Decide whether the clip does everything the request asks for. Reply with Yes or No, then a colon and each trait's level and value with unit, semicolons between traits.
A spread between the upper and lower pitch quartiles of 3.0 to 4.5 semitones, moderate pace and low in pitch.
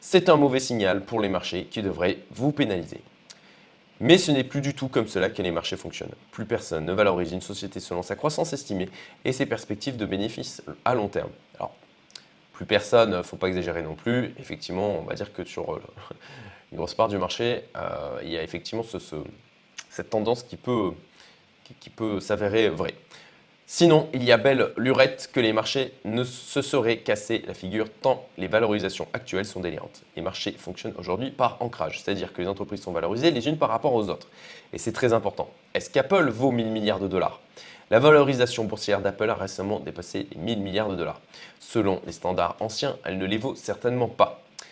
No: average, 5.0 semitones; average, 200 wpm; low, 110 Hz